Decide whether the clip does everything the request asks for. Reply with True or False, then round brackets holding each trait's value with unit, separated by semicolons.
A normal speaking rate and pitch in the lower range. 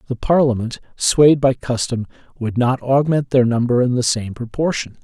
True (165 wpm; 125 Hz)